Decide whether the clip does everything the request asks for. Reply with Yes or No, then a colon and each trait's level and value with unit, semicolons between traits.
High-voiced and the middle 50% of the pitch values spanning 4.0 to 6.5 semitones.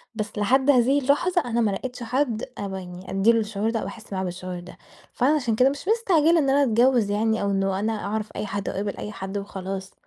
Yes: high, 220 Hz; average, 4.9 semitones